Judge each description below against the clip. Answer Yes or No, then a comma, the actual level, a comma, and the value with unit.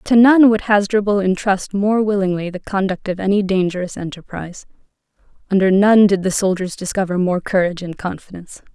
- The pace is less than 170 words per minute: Yes, average, 160 wpm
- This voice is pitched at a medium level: No, high, 195 Hz